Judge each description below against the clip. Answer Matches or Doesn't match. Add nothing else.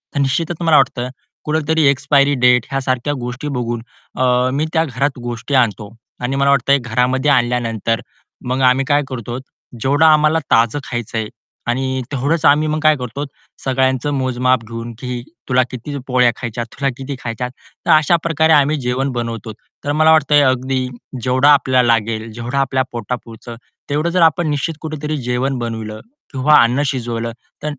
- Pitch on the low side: Matches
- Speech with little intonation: Doesn't match